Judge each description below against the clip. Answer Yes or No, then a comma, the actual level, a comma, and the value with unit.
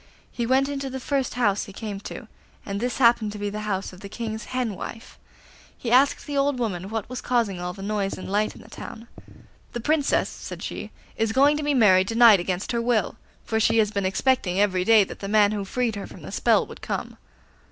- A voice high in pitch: Yes, high, 220 Hz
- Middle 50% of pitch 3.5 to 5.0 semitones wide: Yes, average, 3.8 semitones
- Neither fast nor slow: No, fast, 235 wpm